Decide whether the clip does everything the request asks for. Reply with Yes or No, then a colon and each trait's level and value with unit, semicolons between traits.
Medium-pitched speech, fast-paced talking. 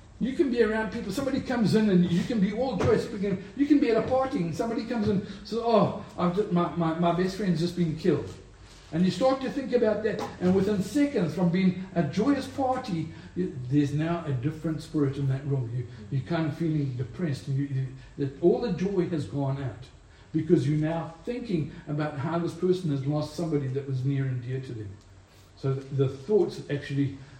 Yes: medium, 170 Hz; fast, 210 wpm